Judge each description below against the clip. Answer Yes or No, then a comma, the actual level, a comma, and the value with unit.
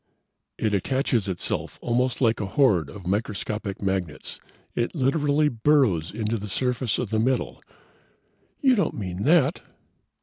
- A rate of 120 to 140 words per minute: Yes, slow, 135 wpm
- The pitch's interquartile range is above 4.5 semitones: Yes, average, 5.3 semitones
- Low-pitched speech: Yes, low, 115 Hz